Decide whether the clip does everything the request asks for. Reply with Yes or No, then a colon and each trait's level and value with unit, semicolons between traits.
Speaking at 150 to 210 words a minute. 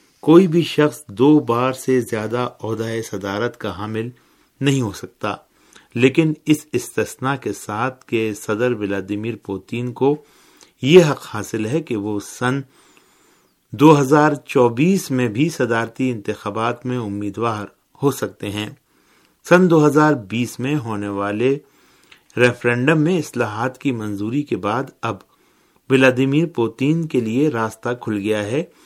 No: average, 135 wpm